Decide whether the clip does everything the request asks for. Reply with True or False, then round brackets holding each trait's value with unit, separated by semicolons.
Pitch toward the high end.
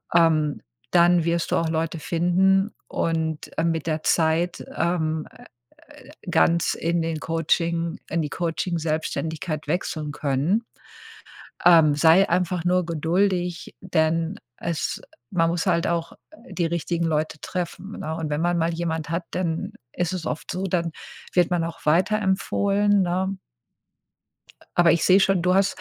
False (170 Hz)